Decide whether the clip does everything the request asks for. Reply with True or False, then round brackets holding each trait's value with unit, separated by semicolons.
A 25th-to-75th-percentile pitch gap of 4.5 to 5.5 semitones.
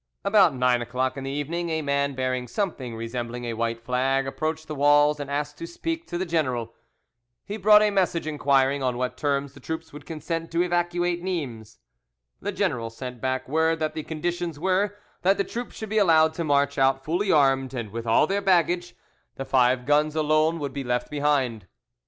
True (4.9 semitones)